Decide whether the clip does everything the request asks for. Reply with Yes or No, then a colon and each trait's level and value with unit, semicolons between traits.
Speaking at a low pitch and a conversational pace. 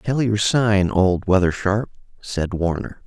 Yes: low, 100 Hz; average, 155 wpm